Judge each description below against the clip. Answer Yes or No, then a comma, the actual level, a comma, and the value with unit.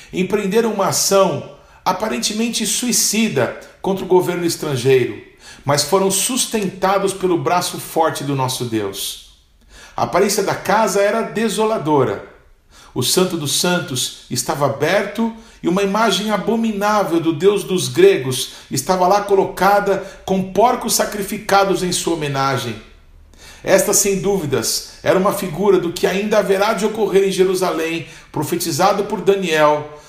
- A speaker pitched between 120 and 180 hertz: No, high, 190 Hz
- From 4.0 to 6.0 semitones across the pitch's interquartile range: Yes, average, 4.4 semitones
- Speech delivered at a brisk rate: No, average, 130 wpm